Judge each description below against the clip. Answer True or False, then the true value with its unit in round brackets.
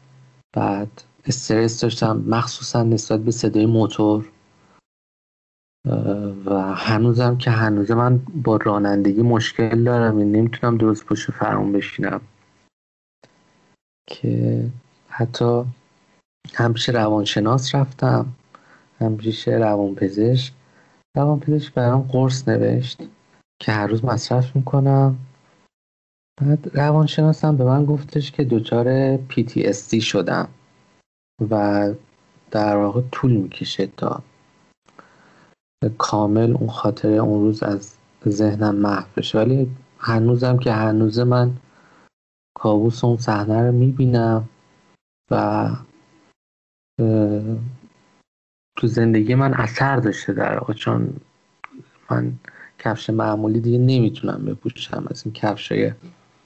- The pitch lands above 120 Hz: False (115 Hz)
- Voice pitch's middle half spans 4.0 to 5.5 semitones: False (3.2 semitones)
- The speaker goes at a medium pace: False (100 wpm)